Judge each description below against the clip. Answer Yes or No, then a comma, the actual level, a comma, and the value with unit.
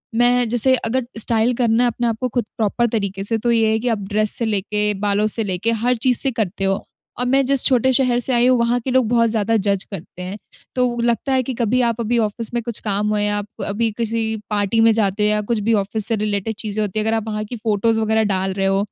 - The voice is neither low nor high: No, high, 225 Hz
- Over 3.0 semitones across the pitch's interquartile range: No, narrow, 2.4 semitones